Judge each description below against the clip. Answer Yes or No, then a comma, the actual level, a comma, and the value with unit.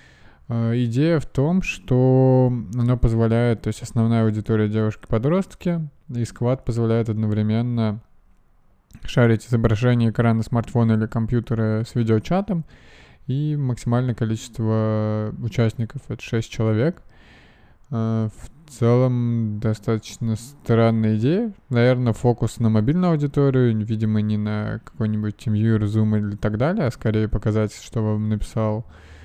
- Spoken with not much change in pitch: Yes, narrow, 2.3 semitones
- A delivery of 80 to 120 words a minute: Yes, average, 115 wpm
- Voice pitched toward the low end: Yes, low, 115 Hz